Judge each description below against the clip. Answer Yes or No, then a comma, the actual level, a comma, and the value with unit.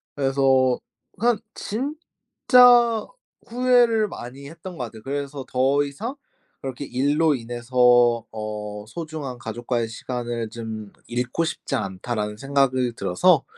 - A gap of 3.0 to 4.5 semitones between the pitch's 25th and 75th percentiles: No, average, 5.1 semitones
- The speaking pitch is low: Yes, low, 130 Hz